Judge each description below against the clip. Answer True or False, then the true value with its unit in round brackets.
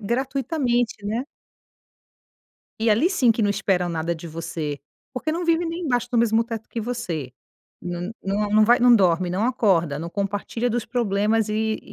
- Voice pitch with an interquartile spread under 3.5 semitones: False (4.8 semitones)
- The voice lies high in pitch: True (215 Hz)